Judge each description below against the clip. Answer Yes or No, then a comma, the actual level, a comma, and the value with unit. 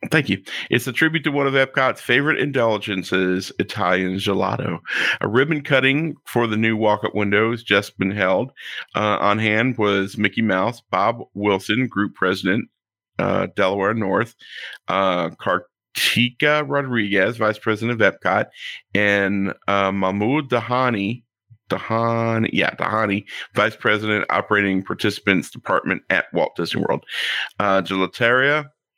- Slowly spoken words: Yes, slow, 130 wpm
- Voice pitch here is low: Yes, low, 105 Hz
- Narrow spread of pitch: No, average, 3.6 semitones